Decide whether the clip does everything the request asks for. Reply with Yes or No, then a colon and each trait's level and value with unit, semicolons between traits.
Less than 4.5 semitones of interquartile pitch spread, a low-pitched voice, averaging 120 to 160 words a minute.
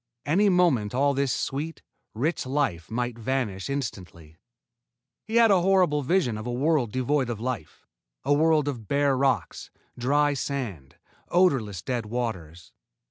No: average, 4.9 semitones; low, 130 Hz; average, 140 wpm